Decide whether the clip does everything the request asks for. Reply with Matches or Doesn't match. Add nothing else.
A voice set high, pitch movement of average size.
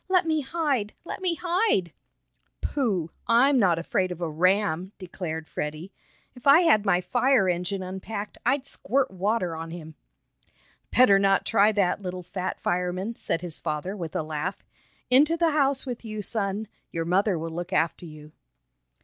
Doesn't match